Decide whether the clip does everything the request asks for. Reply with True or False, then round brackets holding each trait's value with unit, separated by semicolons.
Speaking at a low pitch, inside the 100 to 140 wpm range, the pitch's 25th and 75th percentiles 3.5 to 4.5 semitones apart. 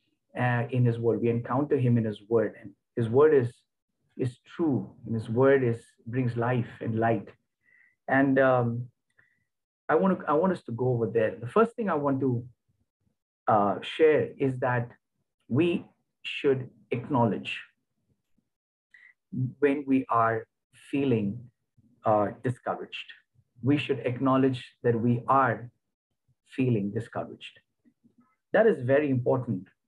False (125 Hz; 135 wpm; 2.8 semitones)